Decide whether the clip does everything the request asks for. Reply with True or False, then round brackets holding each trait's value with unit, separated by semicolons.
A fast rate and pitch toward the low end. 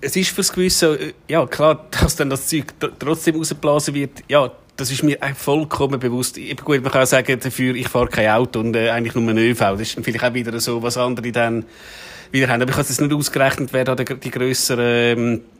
True (225 wpm; 130 Hz)